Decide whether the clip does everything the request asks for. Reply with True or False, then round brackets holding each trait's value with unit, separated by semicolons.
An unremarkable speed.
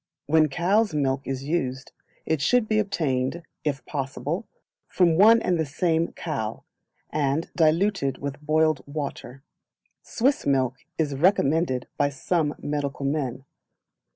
False (125 wpm)